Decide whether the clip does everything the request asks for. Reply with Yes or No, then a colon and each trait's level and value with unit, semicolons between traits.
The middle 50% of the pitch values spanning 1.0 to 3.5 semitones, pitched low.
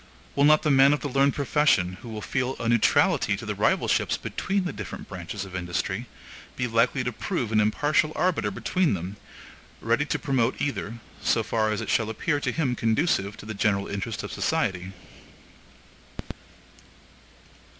No: wide, 5.6 semitones; low, 115 Hz